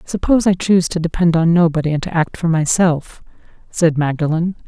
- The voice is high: No, medium, 165 Hz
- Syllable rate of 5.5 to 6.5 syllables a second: Yes, 5.7 syllables/s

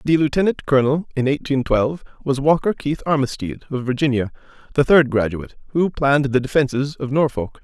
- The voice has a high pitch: No, medium, 140 Hz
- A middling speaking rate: Yes, average, 155 wpm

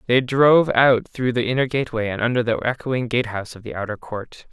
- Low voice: Yes, low, 120 Hz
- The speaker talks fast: Yes, fast, 210 wpm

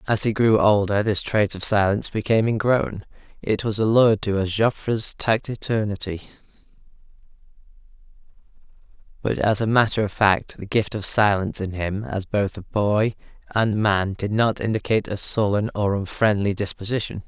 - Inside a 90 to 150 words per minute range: Yes, average, 145 wpm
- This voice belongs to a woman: No, male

